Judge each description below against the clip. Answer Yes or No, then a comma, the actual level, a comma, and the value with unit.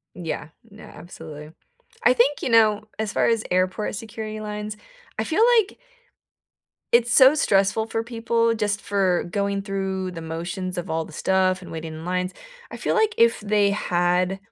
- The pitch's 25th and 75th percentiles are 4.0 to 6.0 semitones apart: No, average, 3.6 semitones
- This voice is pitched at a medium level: No, high, 200 Hz